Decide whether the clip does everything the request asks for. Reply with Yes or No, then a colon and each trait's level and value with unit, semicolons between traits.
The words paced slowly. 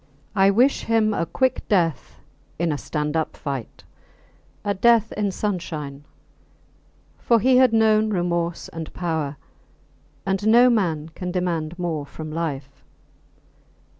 Yes: slow, 130 wpm